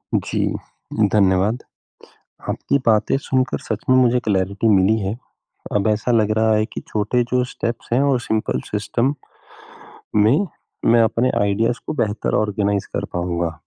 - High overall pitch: No, low, 110 Hz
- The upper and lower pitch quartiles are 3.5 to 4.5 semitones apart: No, average, 2.9 semitones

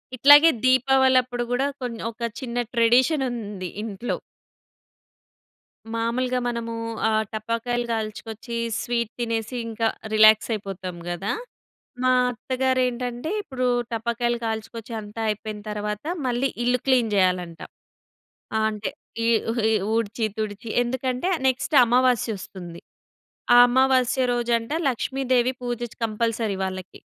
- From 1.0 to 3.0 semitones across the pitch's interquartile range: Yes, average, 2.7 semitones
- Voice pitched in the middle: No, high, 235 Hz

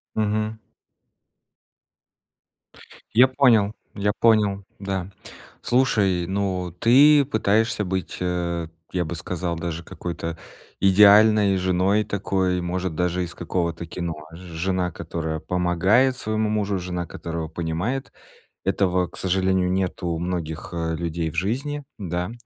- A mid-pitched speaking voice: No, very low, 95 Hz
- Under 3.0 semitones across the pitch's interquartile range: No, average, 3.3 semitones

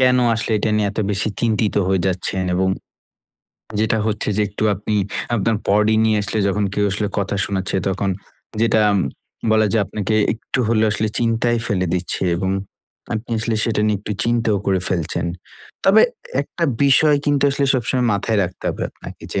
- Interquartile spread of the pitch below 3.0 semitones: Yes, narrow, 2.6 semitones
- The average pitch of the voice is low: Yes, low, 110 Hz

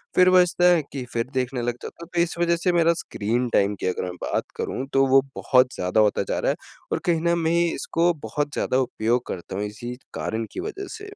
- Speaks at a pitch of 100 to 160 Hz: Yes, low, 135 Hz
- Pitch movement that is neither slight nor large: No, wide, 6.7 semitones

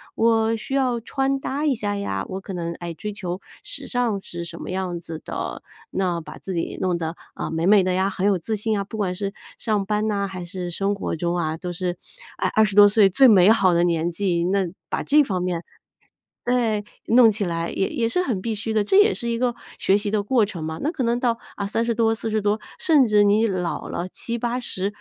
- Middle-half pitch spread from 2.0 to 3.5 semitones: No, average, 4.2 semitones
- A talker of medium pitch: No, high, 205 Hz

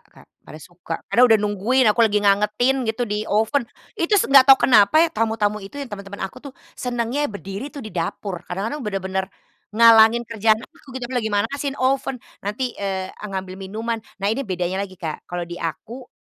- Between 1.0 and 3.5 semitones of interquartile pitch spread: No, average, 4.3 semitones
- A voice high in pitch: Yes, high, 215 Hz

